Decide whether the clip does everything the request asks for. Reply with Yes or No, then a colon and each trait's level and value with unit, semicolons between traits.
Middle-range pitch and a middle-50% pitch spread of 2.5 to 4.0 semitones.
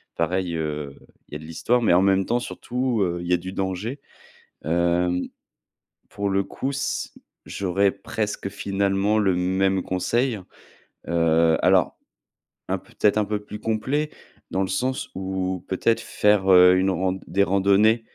No: very low, 95 Hz; average, 2.8 semitones